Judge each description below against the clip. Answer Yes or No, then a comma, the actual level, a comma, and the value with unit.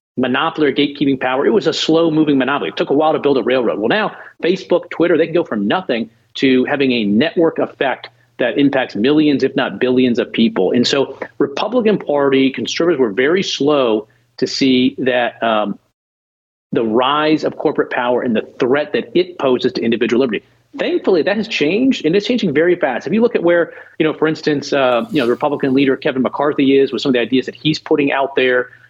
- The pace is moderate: No, fast, 210 wpm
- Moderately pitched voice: Yes, medium, 145 Hz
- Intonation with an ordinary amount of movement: Yes, average, 3.7 semitones